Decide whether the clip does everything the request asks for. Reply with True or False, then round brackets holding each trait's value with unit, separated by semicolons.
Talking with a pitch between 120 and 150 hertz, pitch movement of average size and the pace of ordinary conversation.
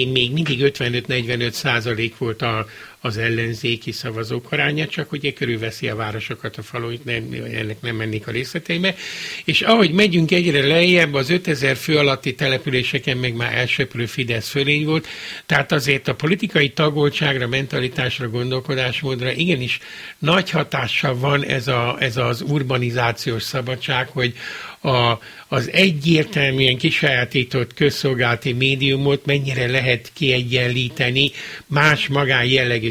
True (130 Hz; 3.1 semitones; 130 wpm)